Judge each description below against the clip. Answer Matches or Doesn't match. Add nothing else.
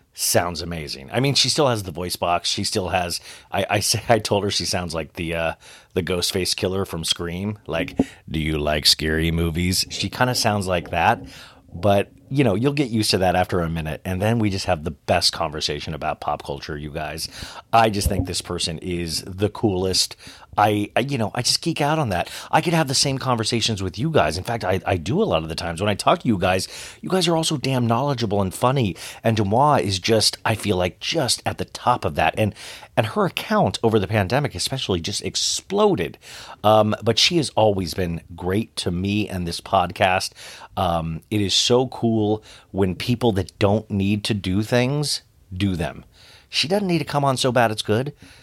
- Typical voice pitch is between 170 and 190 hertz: Doesn't match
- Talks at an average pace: Doesn't match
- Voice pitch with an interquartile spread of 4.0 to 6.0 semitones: Matches